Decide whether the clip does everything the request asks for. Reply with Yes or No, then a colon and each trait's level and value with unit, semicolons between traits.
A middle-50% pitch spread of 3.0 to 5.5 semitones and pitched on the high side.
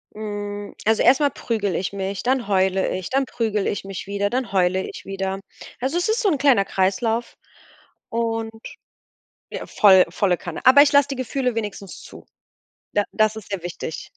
Yes: average, 4.4 semitones; high, 210 Hz